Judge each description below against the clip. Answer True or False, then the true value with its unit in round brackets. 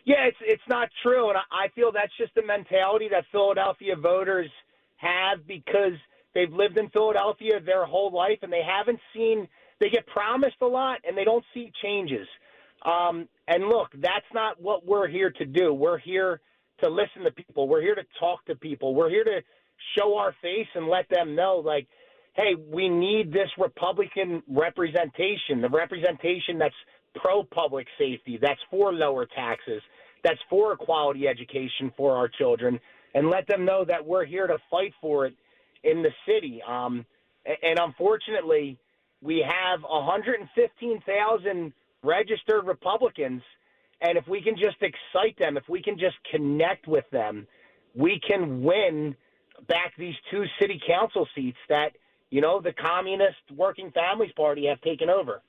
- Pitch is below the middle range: False (190 Hz)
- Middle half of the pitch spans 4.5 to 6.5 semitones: True (4.9 semitones)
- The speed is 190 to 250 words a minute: False (165 wpm)